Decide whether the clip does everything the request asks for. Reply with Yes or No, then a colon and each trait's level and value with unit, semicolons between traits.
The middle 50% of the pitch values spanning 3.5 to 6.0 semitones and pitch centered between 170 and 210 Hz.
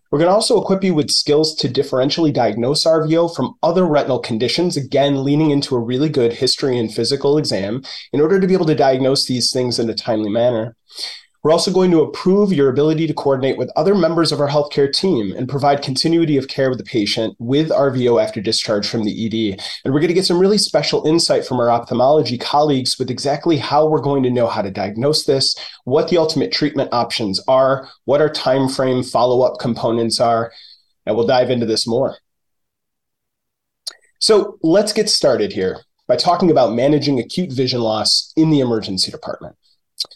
No: average, 4.7 semitones; low, 135 Hz